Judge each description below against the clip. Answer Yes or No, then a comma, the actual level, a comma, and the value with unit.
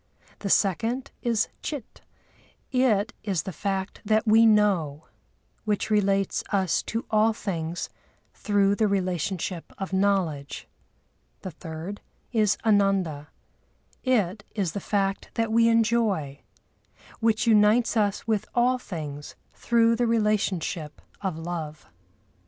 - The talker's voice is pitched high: Yes, high, 200 Hz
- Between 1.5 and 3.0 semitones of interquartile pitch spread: No, average, 3.7 semitones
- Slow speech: Yes, slow, 115 wpm